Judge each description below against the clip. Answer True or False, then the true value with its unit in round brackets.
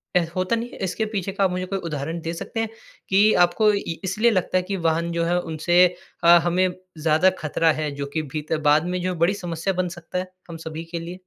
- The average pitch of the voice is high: False (180 Hz)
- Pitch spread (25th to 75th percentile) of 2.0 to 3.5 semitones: True (2.5 semitones)